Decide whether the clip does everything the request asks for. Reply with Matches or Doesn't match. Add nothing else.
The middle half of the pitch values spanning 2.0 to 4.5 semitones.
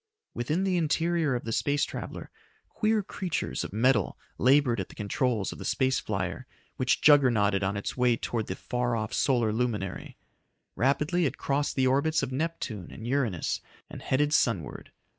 Doesn't match